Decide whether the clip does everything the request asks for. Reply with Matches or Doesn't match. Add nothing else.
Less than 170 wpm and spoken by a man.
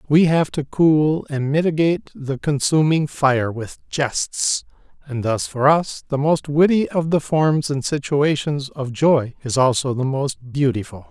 Matches